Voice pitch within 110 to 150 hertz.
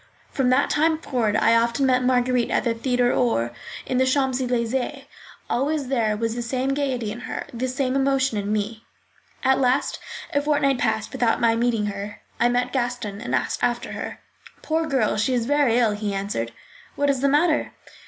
No: high, 245 Hz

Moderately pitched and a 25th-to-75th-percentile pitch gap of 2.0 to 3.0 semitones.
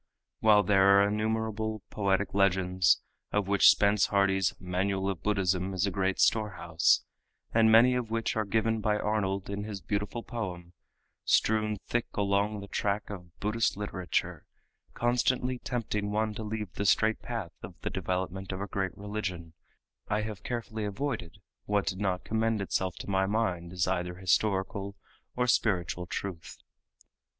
No: low, 100 Hz; narrow, 2.4 semitones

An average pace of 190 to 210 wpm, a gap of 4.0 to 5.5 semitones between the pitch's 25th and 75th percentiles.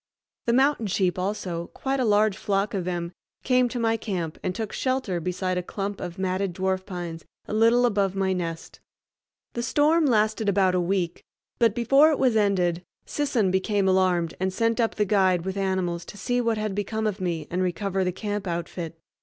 No: average, 195 wpm; average, 3.5 semitones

